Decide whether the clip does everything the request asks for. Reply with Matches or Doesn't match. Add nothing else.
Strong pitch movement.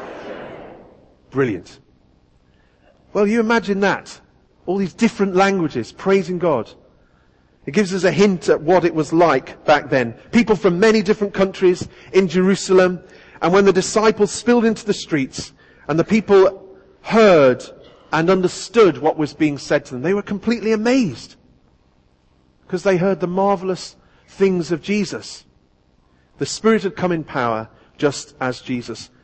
Matches